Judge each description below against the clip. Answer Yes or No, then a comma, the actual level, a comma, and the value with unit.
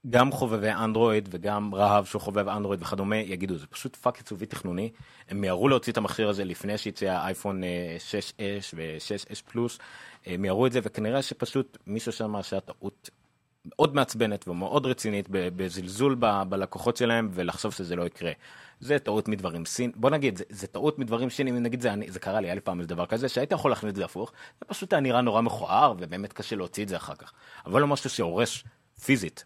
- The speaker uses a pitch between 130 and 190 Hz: No, low, 105 Hz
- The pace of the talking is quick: Yes, fast, 185 wpm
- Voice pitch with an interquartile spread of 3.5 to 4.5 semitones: Yes, average, 4.1 semitones